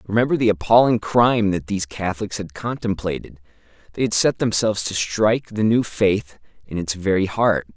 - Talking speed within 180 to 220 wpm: No, average, 170 wpm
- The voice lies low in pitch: Yes, low, 100 Hz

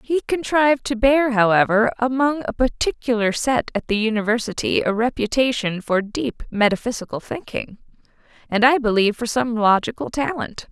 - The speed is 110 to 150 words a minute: Yes, average, 140 wpm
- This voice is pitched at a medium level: No, high, 235 Hz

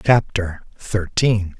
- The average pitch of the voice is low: Yes, low, 100 Hz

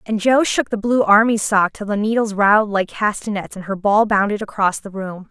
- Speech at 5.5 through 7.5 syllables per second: No, 5.2 syllables/s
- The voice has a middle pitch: No, high, 210 Hz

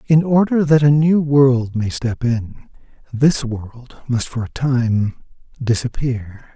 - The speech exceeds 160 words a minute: No, average, 145 wpm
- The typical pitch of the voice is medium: No, low, 130 Hz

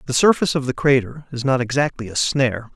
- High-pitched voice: No, low, 135 Hz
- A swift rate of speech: Yes, fast, 220 wpm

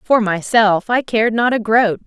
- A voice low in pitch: No, high, 220 Hz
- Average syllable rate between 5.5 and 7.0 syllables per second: No, 4.6 syllables/s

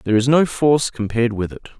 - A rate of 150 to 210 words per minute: No, fast, 235 wpm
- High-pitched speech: No, low, 120 Hz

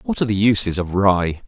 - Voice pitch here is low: Yes, low, 105 Hz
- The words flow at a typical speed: No, fast, 245 wpm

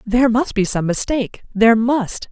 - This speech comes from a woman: Yes, female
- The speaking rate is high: No, average, 180 wpm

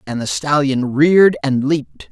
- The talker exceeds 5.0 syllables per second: No, 4.7 syllables/s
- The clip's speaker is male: Yes, male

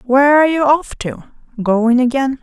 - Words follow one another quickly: No, average, 175 wpm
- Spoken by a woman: Yes, female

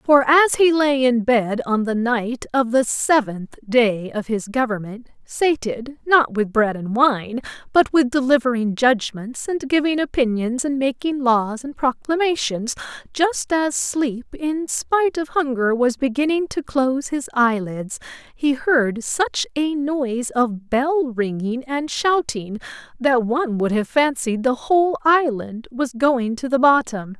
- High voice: Yes, very high, 255 Hz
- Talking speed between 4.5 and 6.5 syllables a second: No, 4.0 syllables/s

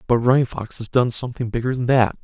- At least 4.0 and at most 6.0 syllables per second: No, 6.3 syllables/s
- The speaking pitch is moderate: No, low, 120 Hz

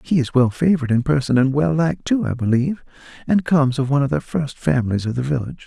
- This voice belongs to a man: Yes, male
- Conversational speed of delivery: No, fast, 245 wpm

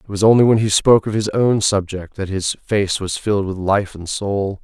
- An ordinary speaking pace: No, fast, 245 wpm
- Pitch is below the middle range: Yes, low, 100 Hz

